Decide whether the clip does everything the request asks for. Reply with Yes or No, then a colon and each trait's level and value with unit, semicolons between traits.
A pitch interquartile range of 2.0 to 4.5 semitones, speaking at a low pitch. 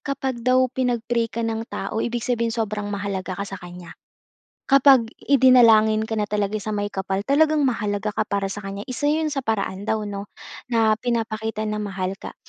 No: average, 3.2 semitones; high, 220 Hz